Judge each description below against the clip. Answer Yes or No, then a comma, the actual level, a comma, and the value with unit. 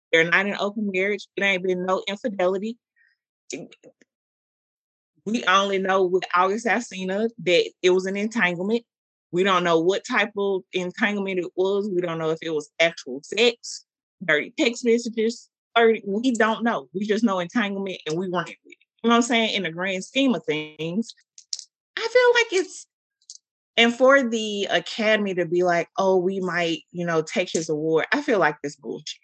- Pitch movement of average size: Yes, average, 4.5 semitones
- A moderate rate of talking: Yes, average, 180 wpm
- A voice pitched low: No, high, 195 Hz